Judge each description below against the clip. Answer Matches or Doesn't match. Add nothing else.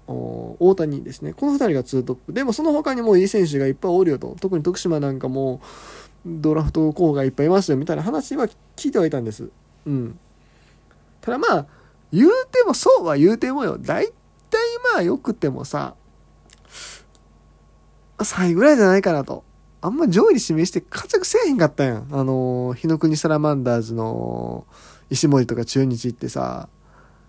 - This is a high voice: Doesn't match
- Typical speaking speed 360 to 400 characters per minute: Doesn't match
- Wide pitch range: Matches